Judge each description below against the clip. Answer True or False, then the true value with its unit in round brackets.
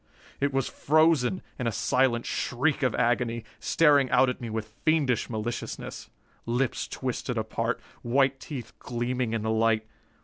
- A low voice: True (125 Hz)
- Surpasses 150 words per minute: False (145 wpm)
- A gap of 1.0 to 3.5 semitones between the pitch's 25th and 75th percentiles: True (2.7 semitones)